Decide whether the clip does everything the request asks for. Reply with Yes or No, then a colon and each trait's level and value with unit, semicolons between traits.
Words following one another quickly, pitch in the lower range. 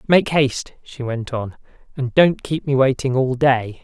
No: average, 190 wpm; low, 130 Hz